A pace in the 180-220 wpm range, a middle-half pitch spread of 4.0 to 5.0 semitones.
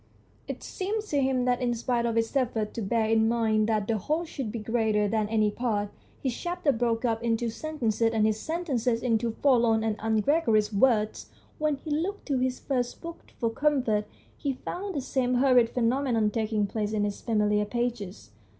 No: average, 185 wpm; average, 3.3 semitones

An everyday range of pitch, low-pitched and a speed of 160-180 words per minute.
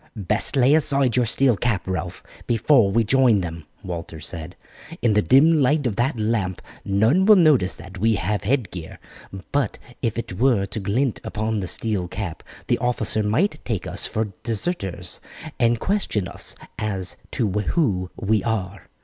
Yes: average, 4.8 semitones; low, 110 Hz; average, 165 wpm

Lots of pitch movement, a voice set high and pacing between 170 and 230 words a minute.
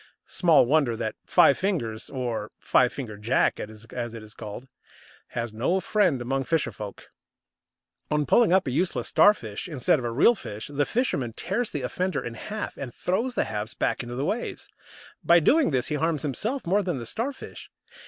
No: wide, 7.7 semitones; low, 135 Hz; average, 185 wpm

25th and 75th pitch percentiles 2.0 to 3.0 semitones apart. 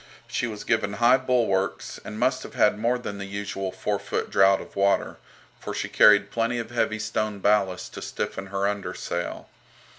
Yes: average, 2.7 semitones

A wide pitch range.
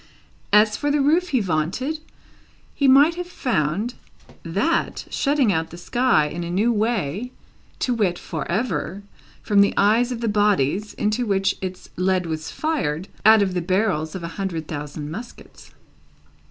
Yes: wide, 6.0 semitones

